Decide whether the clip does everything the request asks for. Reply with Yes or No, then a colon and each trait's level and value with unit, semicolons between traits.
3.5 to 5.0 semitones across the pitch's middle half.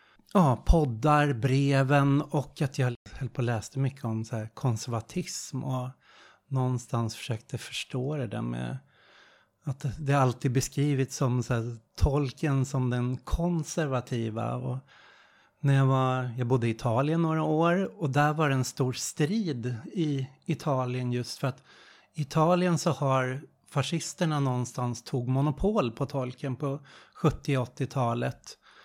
No: average, 3.0 semitones